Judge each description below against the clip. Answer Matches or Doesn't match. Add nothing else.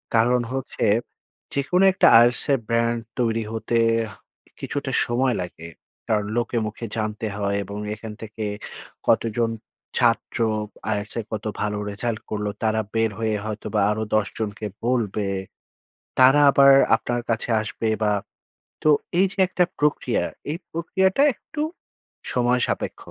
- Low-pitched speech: Matches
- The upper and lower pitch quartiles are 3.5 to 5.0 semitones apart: Doesn't match